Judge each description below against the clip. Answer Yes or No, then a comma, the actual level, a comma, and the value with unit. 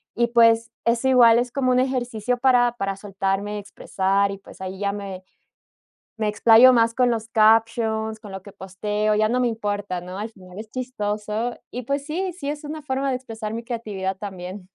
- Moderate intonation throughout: Yes, average, 3.4 semitones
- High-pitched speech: Yes, high, 220 Hz